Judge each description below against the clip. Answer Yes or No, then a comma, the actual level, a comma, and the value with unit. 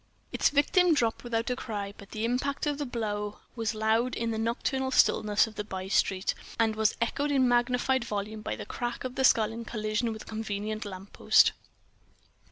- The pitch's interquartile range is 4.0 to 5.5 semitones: No, average, 2.7 semitones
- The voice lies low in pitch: No, high, 225 Hz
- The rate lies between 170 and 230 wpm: Yes, average, 185 wpm